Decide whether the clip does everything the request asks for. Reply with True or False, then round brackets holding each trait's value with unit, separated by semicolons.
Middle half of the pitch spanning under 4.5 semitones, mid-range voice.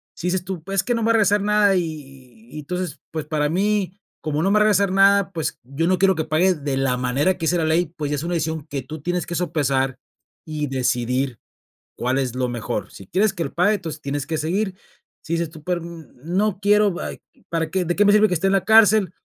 False (4.8 semitones; 170 Hz)